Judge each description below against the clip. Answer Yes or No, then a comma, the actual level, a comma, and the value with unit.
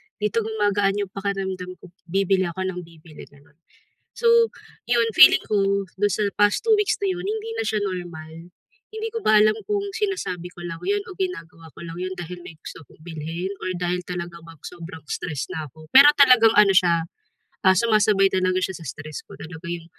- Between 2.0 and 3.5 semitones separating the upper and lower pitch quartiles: No, average, 4.1 semitones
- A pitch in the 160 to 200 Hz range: Yes, medium, 185 Hz